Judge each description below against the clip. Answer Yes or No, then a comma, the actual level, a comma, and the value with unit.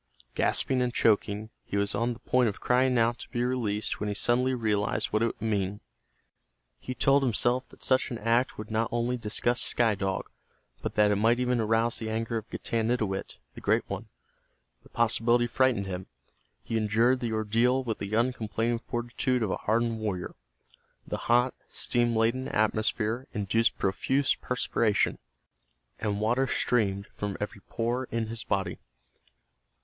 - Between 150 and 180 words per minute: Yes, average, 165 wpm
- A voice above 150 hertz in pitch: No, low, 115 Hz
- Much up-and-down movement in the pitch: No, narrow, 2.4 semitones